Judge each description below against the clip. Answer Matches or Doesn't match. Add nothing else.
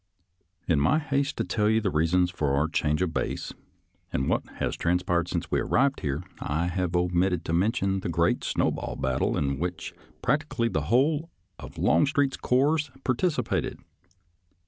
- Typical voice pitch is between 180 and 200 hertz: Doesn't match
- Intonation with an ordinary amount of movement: Doesn't match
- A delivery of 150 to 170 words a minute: Matches